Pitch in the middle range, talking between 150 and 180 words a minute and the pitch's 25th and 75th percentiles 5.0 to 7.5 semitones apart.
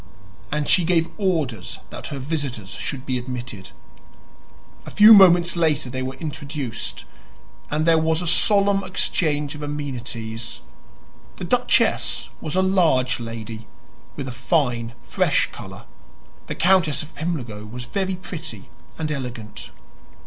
No: medium, 145 Hz; slow, 135 wpm; wide, 5.6 semitones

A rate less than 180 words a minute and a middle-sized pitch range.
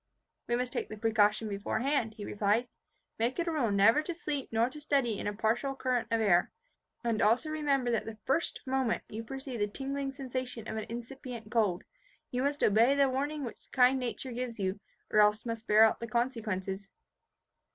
No: average, 190 wpm; average, 3.7 semitones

